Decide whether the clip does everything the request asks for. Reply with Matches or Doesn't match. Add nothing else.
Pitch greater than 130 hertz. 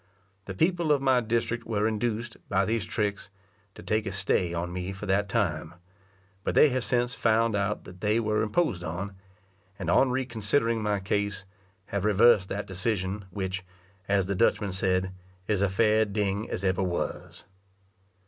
Doesn't match